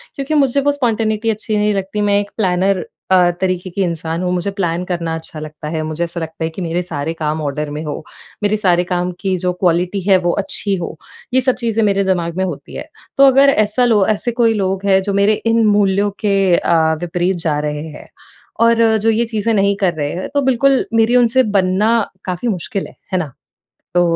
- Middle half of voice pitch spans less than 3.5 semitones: No, average, 3.8 semitones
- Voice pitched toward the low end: No, high, 190 Hz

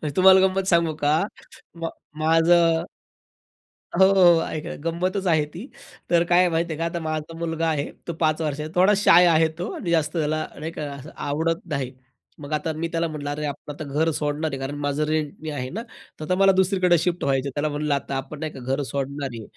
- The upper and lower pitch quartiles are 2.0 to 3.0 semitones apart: Yes, narrow, 2.6 semitones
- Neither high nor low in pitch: Yes, medium, 155 Hz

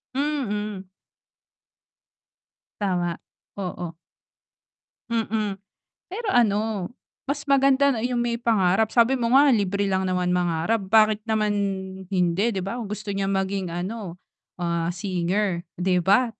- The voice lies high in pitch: Yes, high, 205 Hz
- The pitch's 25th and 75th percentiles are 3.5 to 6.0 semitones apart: Yes, average, 4.1 semitones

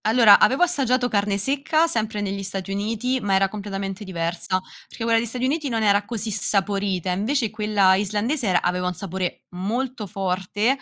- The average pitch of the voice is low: No, high, 205 Hz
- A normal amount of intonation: Yes, average, 3.3 semitones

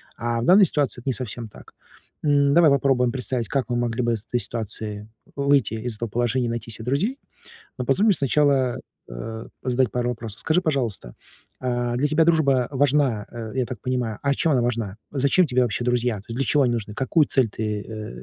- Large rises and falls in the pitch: No, average, 3.5 semitones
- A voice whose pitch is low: Yes, low, 125 Hz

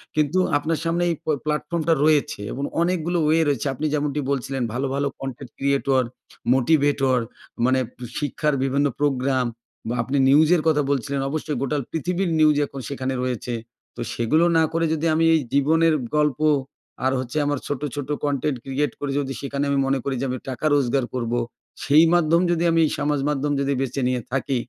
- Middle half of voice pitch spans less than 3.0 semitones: Yes, narrow, 2.6 semitones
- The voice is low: No, medium, 145 Hz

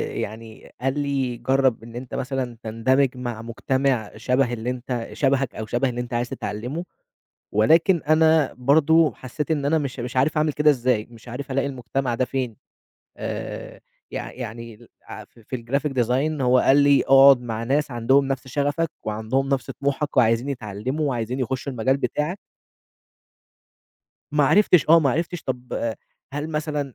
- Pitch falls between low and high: No, low, 130 Hz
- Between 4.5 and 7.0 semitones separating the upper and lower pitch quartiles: No, average, 3.0 semitones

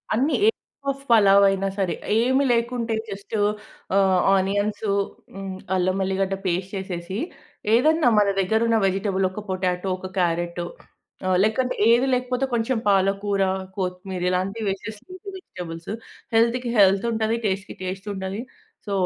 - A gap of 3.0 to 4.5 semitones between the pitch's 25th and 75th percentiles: Yes, average, 3.4 semitones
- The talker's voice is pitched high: Yes, high, 195 Hz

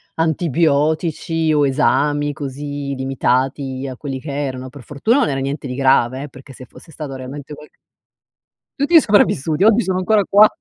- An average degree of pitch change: Yes, average, 3.2 semitones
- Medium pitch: Yes, medium, 145 Hz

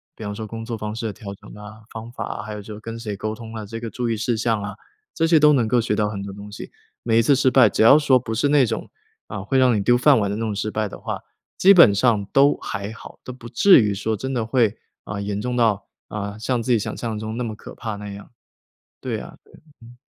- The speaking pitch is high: No, low, 110 Hz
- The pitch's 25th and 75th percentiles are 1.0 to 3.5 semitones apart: Yes, average, 2.7 semitones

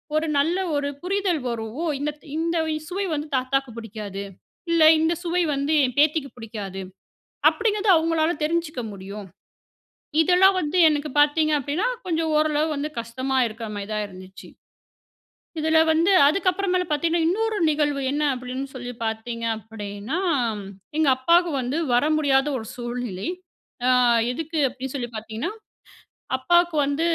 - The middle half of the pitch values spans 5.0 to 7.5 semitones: Yes, wide, 5.6 semitones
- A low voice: No, very high, 290 Hz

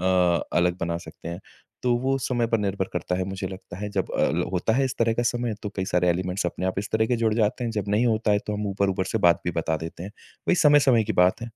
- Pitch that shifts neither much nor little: Yes, average, 4.2 semitones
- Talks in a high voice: No, low, 100 Hz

